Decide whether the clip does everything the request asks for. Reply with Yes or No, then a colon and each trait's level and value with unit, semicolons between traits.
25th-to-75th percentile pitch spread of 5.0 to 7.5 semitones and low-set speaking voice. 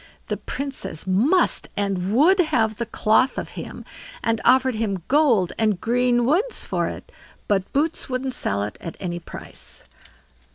No: wide, 5.5 semitones; high, 230 Hz